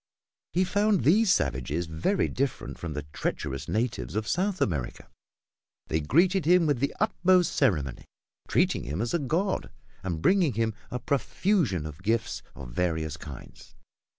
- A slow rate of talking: No, average, 150 wpm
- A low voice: Yes, low, 115 Hz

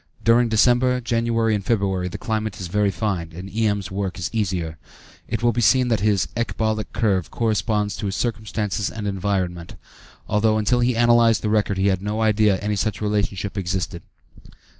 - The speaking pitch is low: Yes, low, 105 Hz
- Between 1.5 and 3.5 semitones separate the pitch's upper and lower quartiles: Yes, average, 2.7 semitones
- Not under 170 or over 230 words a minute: Yes, average, 180 wpm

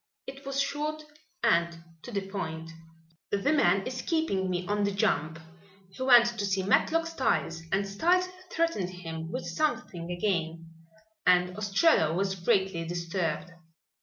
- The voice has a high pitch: Yes, high, 195 Hz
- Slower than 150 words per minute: Yes, average, 140 wpm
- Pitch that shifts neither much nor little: No, wide, 6.5 semitones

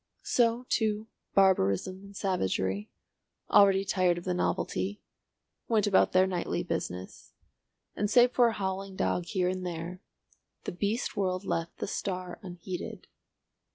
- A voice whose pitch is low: No, high, 190 Hz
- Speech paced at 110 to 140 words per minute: Yes, slow, 135 wpm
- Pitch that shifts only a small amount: Yes, narrow, 2.3 semitones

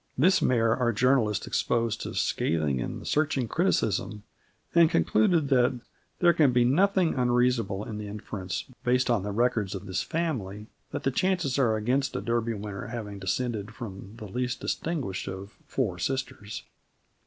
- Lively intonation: No, average, 4.4 semitones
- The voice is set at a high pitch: No, low, 120 Hz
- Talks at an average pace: Yes, average, 155 wpm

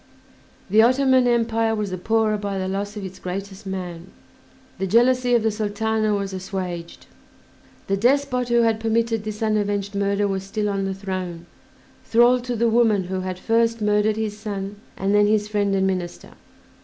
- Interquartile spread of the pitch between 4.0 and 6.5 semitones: No, average, 2.7 semitones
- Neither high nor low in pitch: No, high, 210 Hz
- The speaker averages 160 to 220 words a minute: Yes, average, 175 wpm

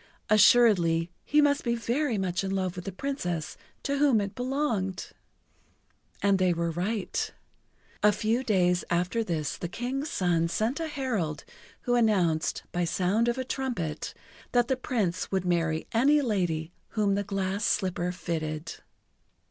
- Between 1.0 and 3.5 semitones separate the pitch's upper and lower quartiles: No, wide, 5.6 semitones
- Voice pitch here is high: Yes, high, 195 Hz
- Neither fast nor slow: Yes, average, 150 wpm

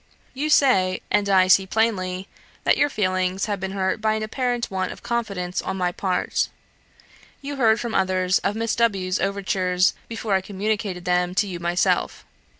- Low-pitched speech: No, high, 195 Hz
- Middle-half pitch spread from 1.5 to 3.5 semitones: Yes, average, 3.0 semitones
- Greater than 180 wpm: No, average, 175 wpm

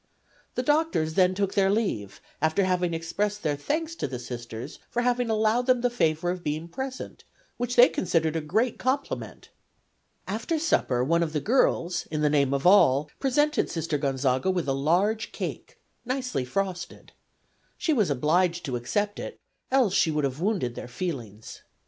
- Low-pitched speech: No, medium, 175 Hz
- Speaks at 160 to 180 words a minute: Yes, average, 170 wpm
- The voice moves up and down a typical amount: No, wide, 7.5 semitones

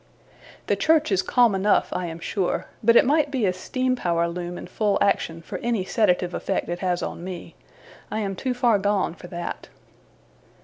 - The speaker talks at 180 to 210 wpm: Yes, average, 190 wpm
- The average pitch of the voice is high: Yes, high, 195 Hz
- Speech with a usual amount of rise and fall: Yes, average, 4.9 semitones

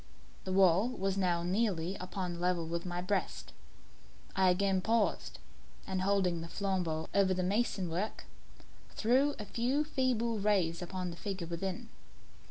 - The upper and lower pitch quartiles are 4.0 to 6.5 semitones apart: No, average, 2.9 semitones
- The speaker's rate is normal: Yes, average, 150 wpm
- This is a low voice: No, high, 190 Hz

